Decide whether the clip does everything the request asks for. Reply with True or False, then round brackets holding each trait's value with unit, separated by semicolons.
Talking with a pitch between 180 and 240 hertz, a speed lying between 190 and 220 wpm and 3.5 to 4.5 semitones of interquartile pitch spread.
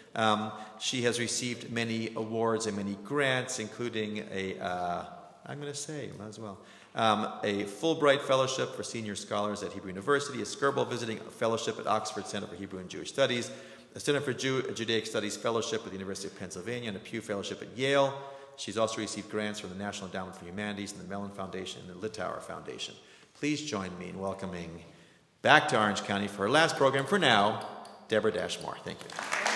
False (105 Hz; 195 wpm; 3.9 semitones)